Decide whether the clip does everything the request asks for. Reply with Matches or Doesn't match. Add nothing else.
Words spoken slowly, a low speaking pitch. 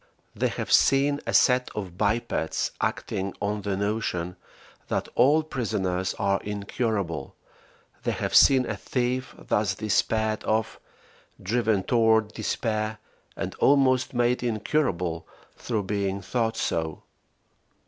Matches